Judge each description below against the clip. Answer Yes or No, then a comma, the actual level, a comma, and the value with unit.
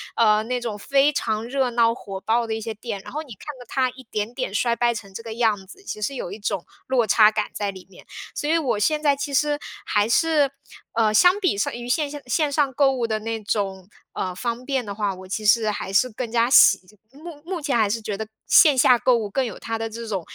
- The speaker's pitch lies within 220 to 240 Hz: Yes, high, 230 Hz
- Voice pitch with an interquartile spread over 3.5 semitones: Yes, average, 4.1 semitones